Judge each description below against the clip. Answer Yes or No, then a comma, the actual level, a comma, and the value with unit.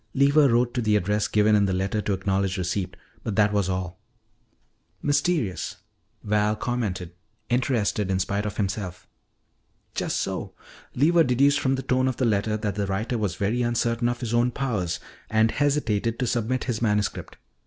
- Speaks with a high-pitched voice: No, low, 110 Hz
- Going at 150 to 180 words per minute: Yes, average, 170 wpm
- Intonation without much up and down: No, average, 3.7 semitones